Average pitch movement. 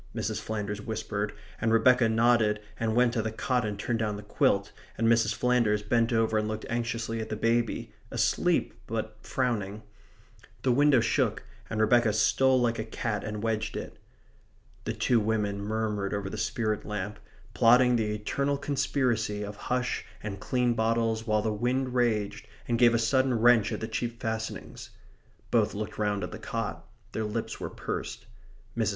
No: narrow, 2.1 semitones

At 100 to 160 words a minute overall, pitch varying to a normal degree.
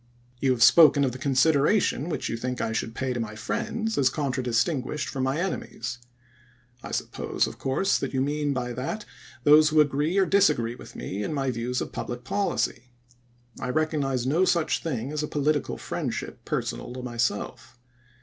No: average, 180 wpm; average, 3.8 semitones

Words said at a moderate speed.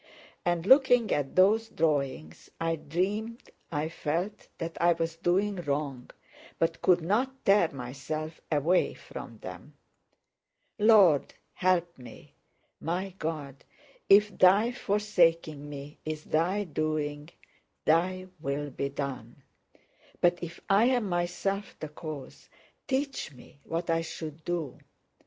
No: slow, 120 wpm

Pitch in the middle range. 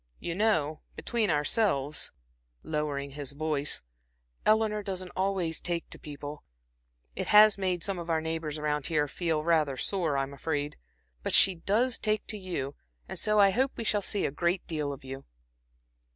Yes: medium, 165 Hz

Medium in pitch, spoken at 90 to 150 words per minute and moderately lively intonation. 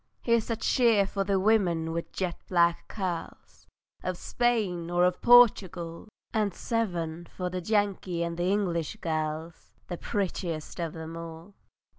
Yes: medium, 180 Hz; average, 140 wpm; average, 3.4 semitones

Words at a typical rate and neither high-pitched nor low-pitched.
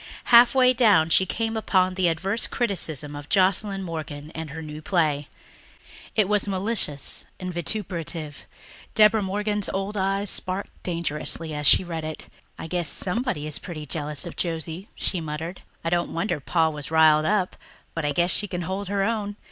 Yes: average, 170 wpm; medium, 180 Hz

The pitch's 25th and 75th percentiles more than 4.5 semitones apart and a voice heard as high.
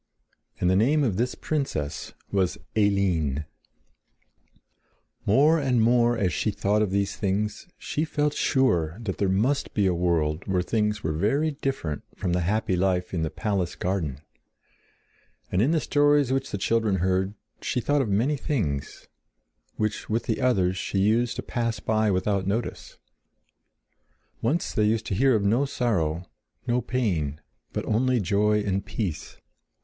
No: average, 4.9 semitones; low, 105 Hz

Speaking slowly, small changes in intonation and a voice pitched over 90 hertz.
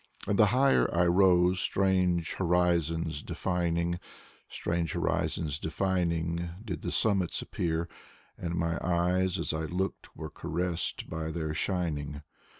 No: slow, 125 wpm; narrow, 1.8 semitones; very low, 85 Hz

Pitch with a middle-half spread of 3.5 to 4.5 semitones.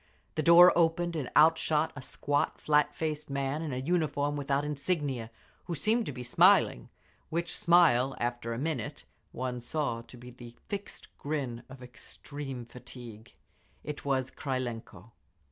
Yes: average, 4.0 semitones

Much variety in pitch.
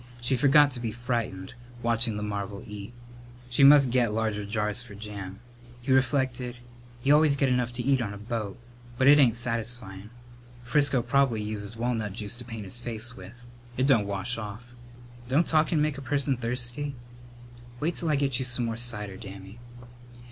No: average, 3.8 semitones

